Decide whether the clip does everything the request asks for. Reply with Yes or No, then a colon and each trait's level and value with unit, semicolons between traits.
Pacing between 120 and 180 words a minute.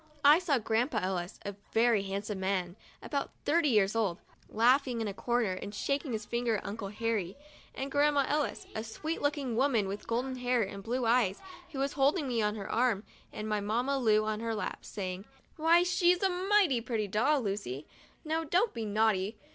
No: average, 190 wpm